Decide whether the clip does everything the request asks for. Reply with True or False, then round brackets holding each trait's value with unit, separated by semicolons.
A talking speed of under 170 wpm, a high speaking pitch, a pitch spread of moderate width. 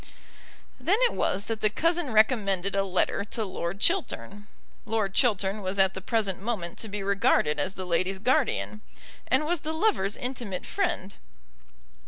True (160 wpm; 205 Hz; 4.7 semitones)